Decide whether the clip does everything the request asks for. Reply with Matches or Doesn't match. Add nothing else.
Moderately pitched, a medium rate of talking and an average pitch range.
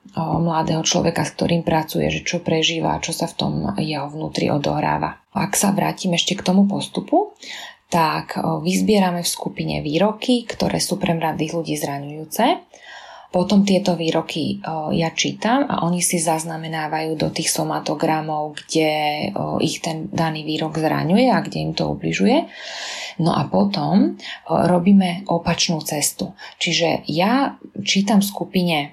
Matches